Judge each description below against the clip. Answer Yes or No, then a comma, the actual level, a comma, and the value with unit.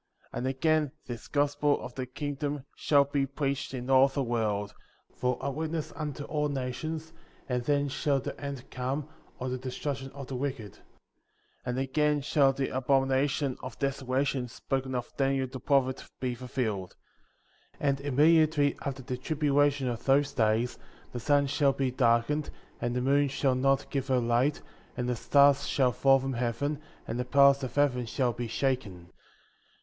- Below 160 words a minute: No, average, 175 wpm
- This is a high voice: No, low, 135 Hz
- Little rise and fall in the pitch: Yes, narrow, 2.2 semitones